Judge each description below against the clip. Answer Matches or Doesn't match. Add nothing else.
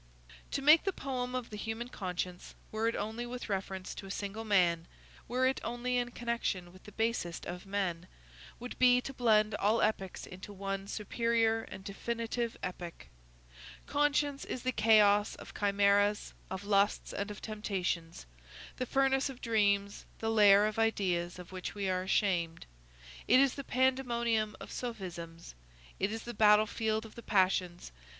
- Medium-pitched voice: Doesn't match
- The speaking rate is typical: Matches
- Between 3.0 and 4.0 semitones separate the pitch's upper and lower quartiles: Matches